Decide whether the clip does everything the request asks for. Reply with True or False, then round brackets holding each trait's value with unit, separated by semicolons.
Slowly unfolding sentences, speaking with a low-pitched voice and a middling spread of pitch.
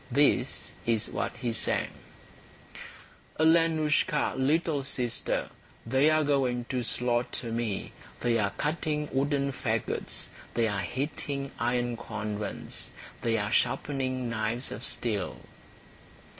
True (110 wpm; 125 Hz; 3.7 semitones)